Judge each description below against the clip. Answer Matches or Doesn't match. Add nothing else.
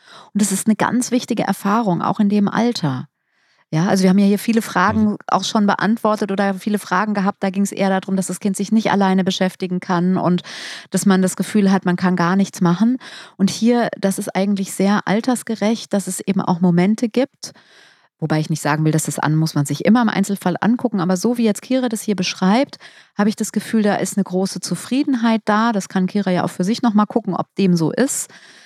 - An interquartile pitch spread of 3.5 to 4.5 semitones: Doesn't match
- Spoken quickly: Matches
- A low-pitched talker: Doesn't match